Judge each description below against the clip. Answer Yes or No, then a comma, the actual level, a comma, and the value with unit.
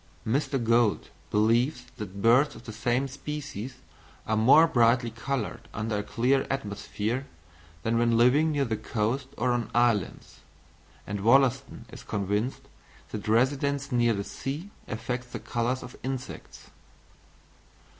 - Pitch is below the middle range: Yes, low, 120 Hz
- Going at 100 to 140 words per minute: Yes, slow, 135 wpm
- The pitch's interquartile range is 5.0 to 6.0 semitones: No, average, 3.4 semitones